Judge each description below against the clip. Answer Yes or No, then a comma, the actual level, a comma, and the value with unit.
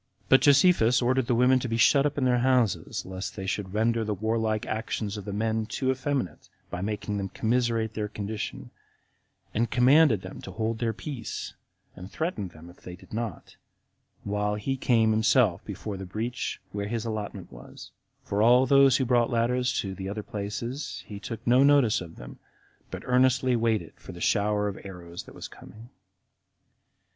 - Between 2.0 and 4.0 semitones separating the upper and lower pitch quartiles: Yes, average, 3.5 semitones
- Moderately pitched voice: No, low, 110 Hz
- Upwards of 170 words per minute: Yes, average, 180 wpm